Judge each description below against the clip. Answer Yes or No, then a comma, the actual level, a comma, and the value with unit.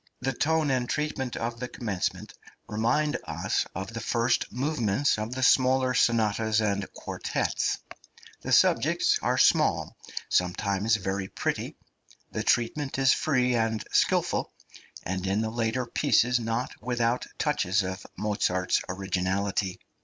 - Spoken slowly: Yes, slow, 130 wpm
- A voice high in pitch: No, low, 115 Hz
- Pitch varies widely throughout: No, average, 4.1 semitones